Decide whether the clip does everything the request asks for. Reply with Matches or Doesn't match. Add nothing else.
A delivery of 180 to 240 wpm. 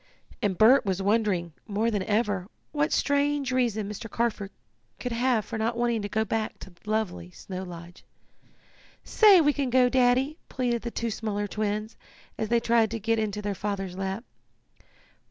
Doesn't match